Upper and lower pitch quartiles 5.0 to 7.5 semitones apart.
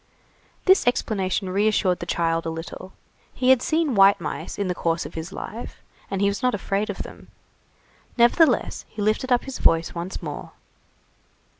Yes: wide, 5.4 semitones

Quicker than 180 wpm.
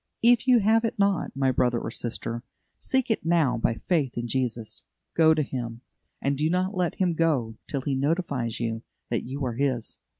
Yes: average, 195 wpm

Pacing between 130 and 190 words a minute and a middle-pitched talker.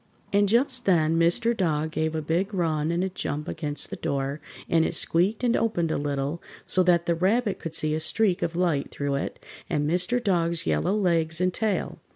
No: average, 200 wpm; medium, 170 Hz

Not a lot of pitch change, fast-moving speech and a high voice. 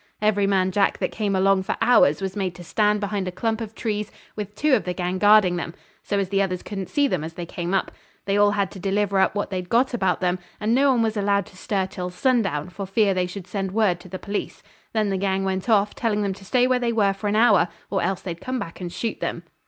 Yes: narrow, 2.3 semitones; fast, 265 wpm; high, 200 Hz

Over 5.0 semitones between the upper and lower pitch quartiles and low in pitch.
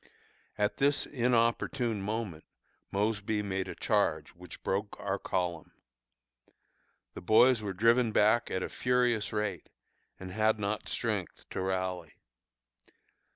No: average, 3.5 semitones; low, 105 Hz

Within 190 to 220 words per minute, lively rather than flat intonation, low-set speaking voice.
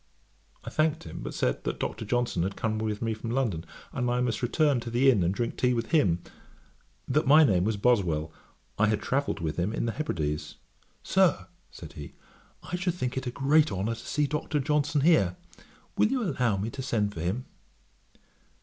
Yes: average, 200 wpm; wide, 6.2 semitones; low, 120 Hz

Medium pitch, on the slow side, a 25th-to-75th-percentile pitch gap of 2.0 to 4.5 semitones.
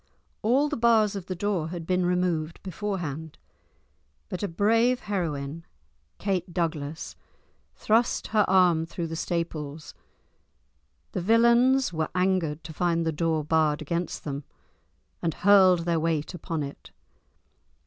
Yes: medium, 175 Hz; slow, 130 wpm; average, 4.0 semitones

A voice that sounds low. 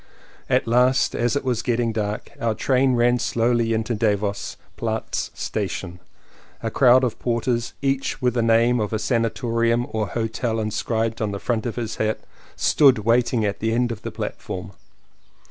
Yes: low, 115 Hz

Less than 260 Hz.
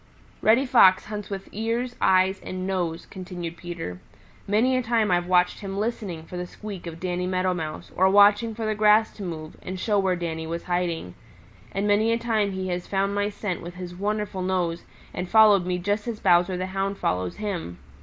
Yes: high, 190 Hz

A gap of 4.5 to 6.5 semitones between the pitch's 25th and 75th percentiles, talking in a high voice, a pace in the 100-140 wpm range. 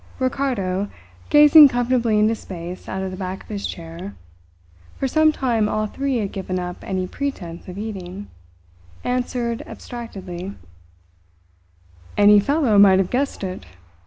Yes: average, 5.0 semitones; high, 205 Hz; slow, 135 wpm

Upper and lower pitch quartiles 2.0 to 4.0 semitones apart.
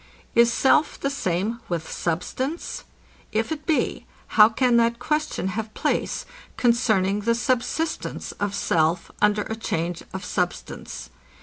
No: average, 4.8 semitones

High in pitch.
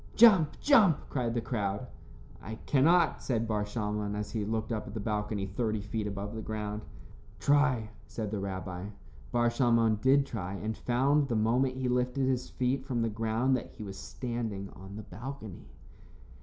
No: low, 115 Hz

